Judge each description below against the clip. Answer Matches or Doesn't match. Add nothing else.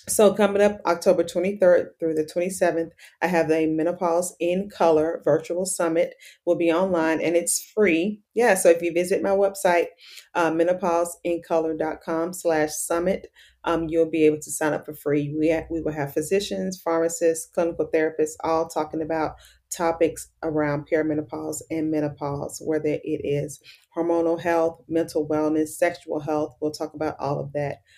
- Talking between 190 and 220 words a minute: Doesn't match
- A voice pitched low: Doesn't match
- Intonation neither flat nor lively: Doesn't match